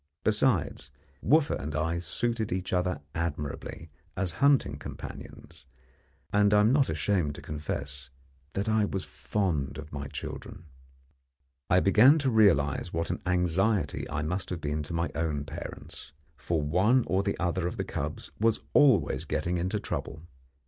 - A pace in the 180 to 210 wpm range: No, average, 155 wpm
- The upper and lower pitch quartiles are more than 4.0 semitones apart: Yes, average, 5.3 semitones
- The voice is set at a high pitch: No, very low, 90 Hz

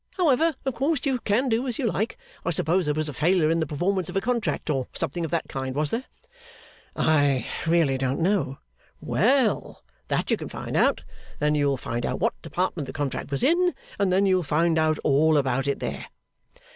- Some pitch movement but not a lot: No, wide, 7.2 semitones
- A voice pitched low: No, medium, 165 Hz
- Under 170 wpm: No, fast, 205 wpm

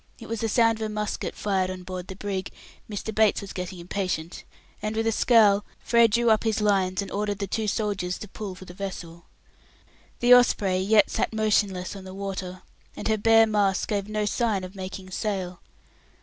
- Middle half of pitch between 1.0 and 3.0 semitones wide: Yes, narrow, 2.6 semitones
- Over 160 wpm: Yes, average, 200 wpm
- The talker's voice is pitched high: Yes, high, 200 Hz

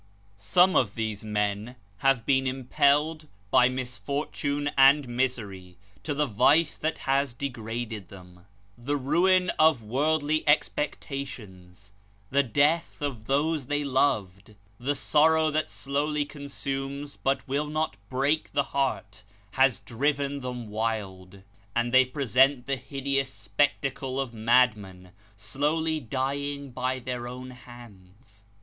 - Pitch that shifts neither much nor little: Yes, average, 4.2 semitones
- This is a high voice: No, low, 130 Hz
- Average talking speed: No, slow, 120 wpm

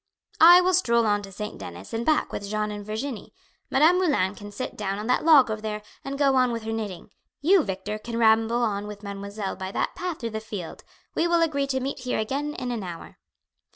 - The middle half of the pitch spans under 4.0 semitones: No, average, 5.1 semitones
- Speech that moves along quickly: Yes, fast, 225 wpm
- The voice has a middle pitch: No, high, 225 Hz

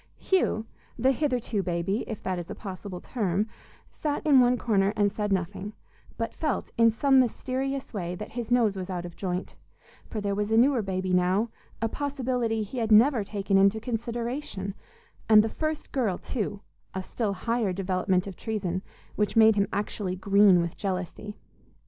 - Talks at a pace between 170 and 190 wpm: Yes, average, 175 wpm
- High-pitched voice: Yes, high, 210 Hz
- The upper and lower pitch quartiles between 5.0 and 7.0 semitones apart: No, average, 3.9 semitones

